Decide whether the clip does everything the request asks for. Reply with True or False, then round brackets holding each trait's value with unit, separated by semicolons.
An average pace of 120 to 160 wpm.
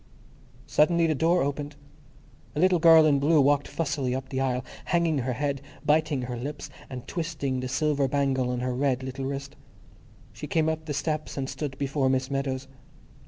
False (180 wpm)